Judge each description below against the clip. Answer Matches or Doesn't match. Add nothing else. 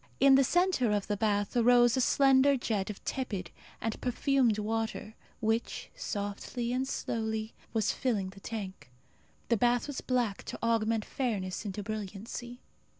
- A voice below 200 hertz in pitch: Doesn't match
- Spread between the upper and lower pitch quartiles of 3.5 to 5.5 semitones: Doesn't match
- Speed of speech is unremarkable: Matches